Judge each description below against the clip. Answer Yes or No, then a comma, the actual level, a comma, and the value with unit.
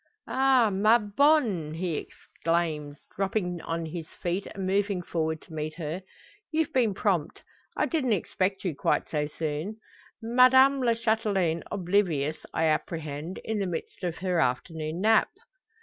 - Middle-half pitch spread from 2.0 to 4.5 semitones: No, average, 5.2 semitones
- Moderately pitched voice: Yes, medium, 180 Hz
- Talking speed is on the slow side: No, average, 145 wpm